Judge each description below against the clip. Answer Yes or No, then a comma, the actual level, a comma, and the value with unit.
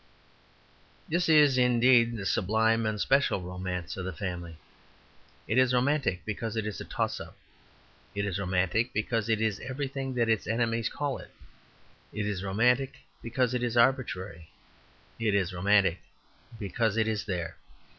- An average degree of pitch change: Yes, average, 4.4 semitones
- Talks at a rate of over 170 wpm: No, average, 155 wpm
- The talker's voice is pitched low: Yes, low, 110 Hz